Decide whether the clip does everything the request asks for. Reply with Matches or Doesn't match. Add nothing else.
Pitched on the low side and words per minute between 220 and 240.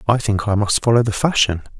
Matches